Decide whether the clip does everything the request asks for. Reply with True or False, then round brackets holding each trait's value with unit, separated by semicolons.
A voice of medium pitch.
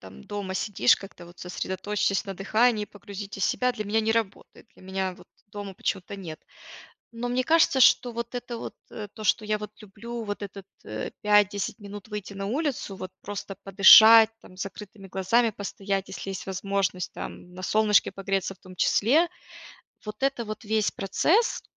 False (205 Hz)